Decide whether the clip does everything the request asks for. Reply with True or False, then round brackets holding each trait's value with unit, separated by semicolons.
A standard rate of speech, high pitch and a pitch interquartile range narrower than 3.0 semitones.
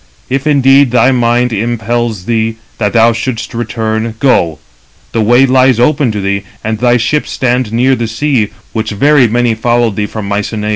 False (175 wpm; 120 Hz; 2.4 semitones)